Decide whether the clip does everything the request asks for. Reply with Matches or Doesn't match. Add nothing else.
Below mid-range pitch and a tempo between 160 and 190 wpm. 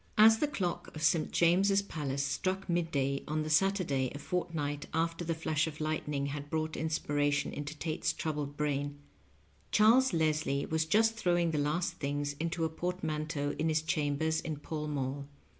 Doesn't match